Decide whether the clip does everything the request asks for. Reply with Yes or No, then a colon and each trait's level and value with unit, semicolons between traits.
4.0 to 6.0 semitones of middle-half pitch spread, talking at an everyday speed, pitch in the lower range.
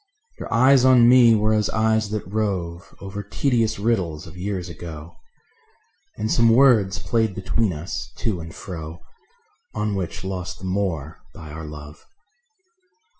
Yes: average, 4.6 semitones; average, 145 wpm; very low, 95 Hz